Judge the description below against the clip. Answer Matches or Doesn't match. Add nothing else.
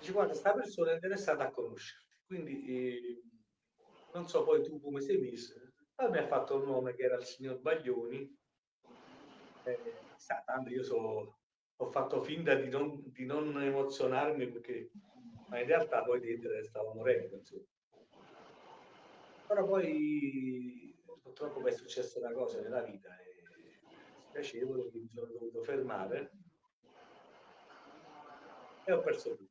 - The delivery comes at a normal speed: Matches